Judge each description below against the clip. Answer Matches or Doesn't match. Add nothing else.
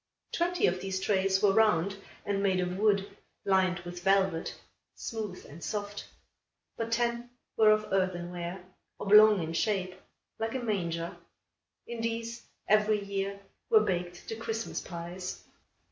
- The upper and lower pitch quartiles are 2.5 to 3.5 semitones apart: Matches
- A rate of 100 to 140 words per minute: Matches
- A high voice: Matches